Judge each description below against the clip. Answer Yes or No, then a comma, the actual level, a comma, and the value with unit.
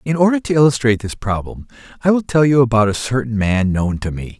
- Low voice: Yes, low, 120 Hz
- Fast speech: Yes, fast, 230 wpm